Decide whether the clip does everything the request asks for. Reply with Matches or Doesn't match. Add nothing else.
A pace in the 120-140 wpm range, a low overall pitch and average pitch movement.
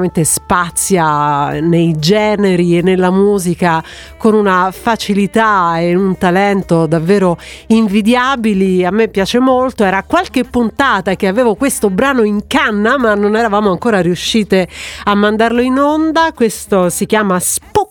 Doesn't match